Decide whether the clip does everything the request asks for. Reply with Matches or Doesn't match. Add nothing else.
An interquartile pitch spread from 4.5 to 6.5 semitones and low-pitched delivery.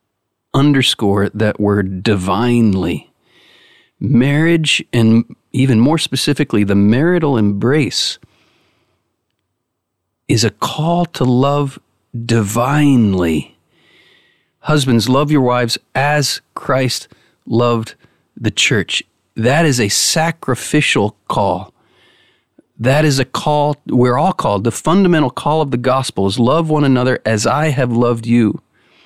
Matches